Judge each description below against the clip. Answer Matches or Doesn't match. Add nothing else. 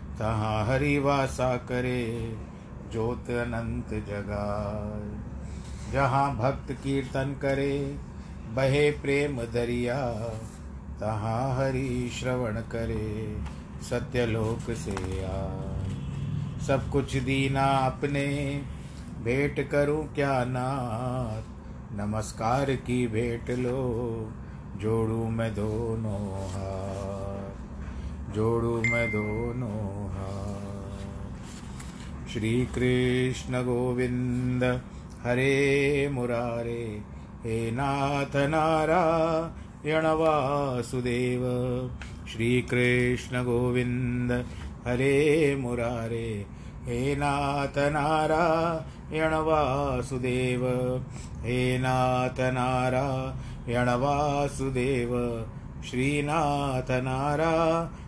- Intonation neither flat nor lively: Matches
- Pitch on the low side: Matches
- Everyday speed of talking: Doesn't match